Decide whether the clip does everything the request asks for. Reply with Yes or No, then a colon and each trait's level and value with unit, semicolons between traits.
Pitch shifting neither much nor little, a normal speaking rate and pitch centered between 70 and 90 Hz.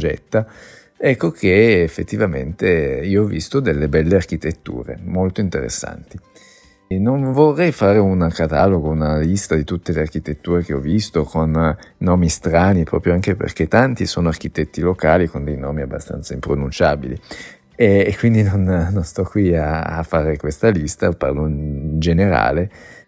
Yes: average, 3.9 semitones; average, 150 wpm; very low, 85 Hz